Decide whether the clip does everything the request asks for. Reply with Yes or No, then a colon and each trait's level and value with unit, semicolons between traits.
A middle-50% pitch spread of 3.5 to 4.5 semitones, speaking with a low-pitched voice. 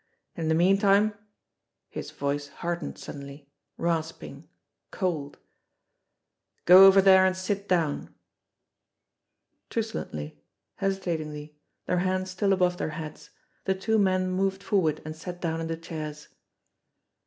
No: average, 3.8 semitones; medium, 175 Hz